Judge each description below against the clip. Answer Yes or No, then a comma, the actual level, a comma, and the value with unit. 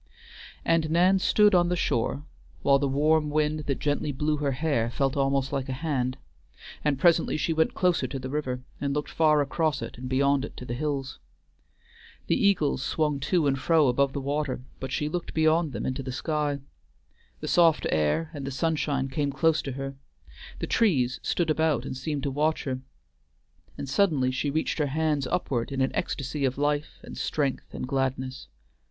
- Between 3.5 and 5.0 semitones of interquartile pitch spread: No, average, 2.8 semitones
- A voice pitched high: No, medium, 145 Hz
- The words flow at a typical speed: Yes, average, 190 wpm